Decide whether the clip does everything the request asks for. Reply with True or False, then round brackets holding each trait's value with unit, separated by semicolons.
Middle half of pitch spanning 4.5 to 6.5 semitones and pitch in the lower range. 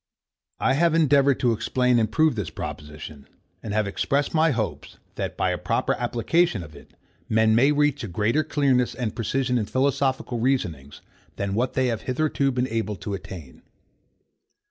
True (4.9 semitones; 125 Hz)